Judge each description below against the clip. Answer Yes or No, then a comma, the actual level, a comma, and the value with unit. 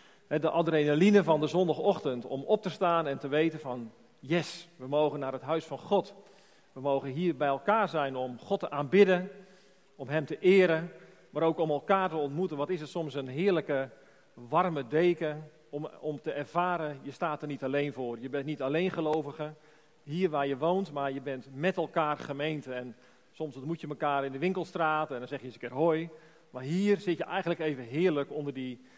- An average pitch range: Yes, average, 3.6 semitones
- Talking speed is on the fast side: Yes, fast, 205 wpm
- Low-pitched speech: No, medium, 155 Hz